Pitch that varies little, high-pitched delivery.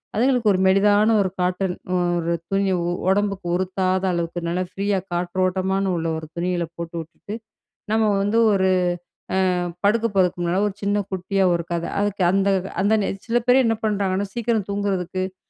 Yes: narrow, 2.1 semitones; high, 195 Hz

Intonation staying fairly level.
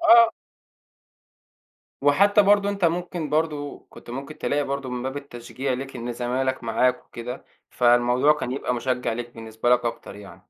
No: average, 3.6 semitones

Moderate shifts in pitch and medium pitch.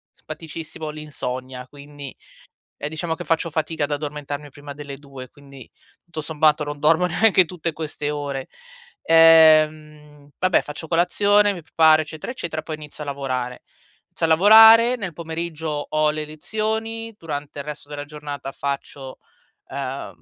No: narrow, 2.3 semitones; medium, 150 Hz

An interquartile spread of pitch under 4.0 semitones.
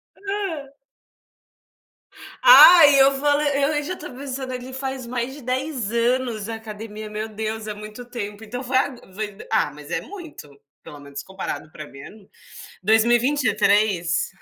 No: average, 4.3 semitones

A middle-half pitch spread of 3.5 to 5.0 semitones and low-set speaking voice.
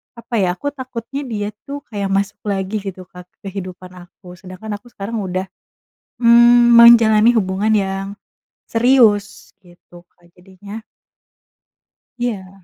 No: average, 3.8 semitones; high, 205 Hz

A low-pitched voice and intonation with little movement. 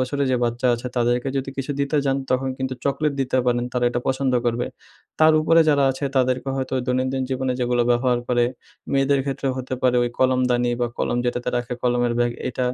Yes: low, 130 Hz; narrow, 1.7 semitones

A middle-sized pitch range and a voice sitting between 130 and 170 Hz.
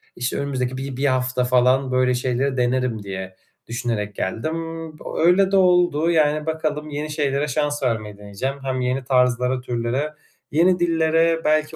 Yes: average, 3.5 semitones; low, 135 Hz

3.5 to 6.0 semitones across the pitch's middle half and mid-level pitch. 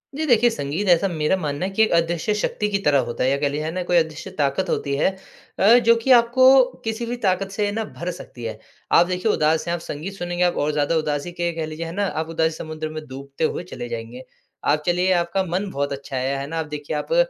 Yes: average, 4.5 semitones; medium, 165 Hz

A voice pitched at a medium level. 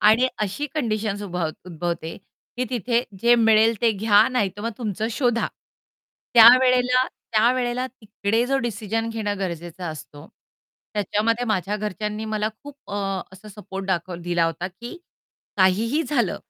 No: high, 215 Hz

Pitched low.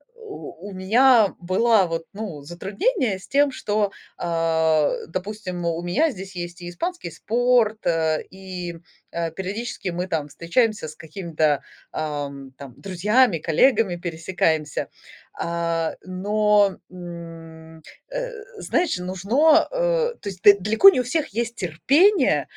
No: medium, 185 Hz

